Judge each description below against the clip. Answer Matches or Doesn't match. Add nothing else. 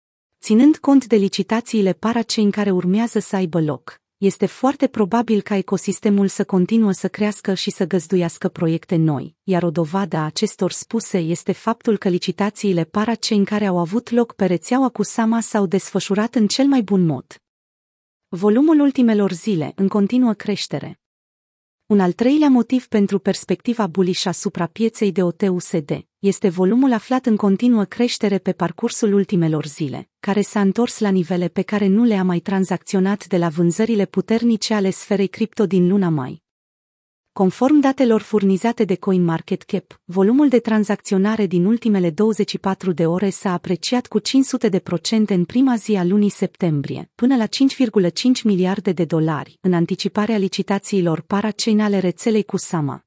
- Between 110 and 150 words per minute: Doesn't match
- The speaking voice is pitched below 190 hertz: Doesn't match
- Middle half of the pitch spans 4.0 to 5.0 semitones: Doesn't match